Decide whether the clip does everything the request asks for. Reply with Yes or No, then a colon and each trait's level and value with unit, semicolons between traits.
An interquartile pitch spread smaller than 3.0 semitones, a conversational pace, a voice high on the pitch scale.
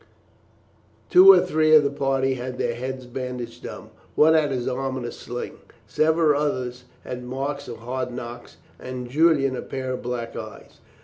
No: narrow, 2.6 semitones; average, 175 wpm; low, 130 Hz